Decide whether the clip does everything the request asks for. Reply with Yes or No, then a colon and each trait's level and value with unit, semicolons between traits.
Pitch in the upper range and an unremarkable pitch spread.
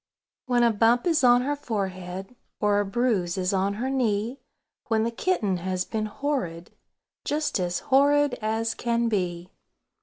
Yes: high, 220 Hz; average, 4.7 semitones